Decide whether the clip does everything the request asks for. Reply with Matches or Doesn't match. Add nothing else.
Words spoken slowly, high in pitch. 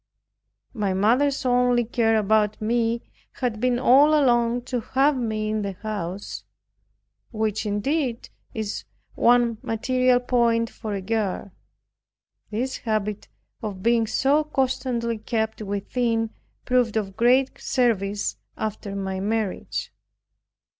Matches